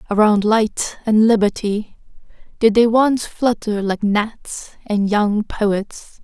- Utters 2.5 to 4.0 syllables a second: Yes, 3.3 syllables/s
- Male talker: No, female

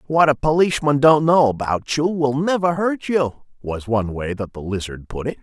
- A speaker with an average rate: No, fast, 210 wpm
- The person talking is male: Yes, male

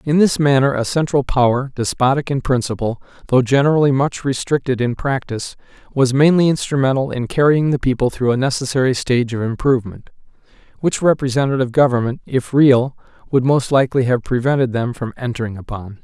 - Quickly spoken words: No, average, 155 wpm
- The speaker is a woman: No, male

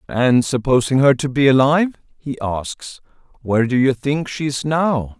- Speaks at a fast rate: No, average, 175 wpm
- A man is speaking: Yes, male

